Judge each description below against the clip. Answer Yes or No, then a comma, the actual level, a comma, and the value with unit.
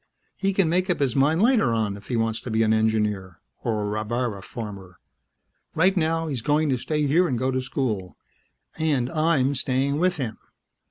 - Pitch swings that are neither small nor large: No, wide, 6.2 semitones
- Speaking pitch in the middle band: No, low, 130 Hz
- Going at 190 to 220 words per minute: Yes, average, 195 wpm